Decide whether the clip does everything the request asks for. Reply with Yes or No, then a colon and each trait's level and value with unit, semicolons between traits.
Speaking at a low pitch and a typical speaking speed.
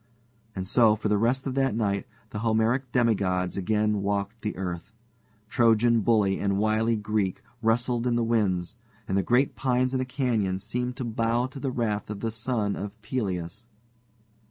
Yes: low, 110 Hz; average, 175 wpm